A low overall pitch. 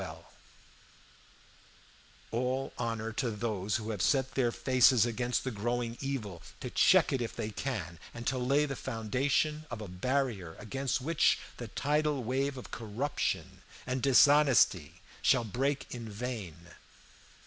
Yes: low, 125 Hz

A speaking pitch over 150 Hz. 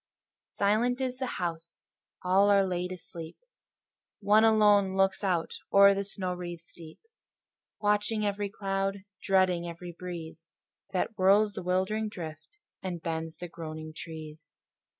Yes: medium, 185 Hz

